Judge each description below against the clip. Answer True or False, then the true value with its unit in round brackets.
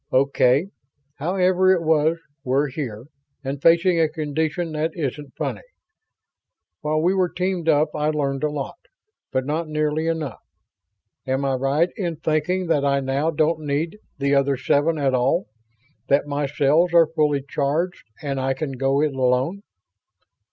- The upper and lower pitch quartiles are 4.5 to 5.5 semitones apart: False (3.1 semitones)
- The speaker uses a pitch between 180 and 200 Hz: False (150 Hz)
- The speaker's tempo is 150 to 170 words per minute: True (155 wpm)